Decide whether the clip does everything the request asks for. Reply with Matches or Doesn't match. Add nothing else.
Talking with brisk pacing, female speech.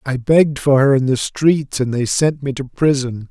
Doesn't match